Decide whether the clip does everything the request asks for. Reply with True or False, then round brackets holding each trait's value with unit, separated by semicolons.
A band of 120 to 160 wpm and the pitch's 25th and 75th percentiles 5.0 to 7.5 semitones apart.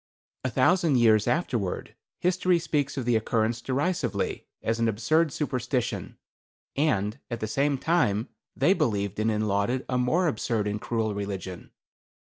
True (145 wpm; 5.4 semitones)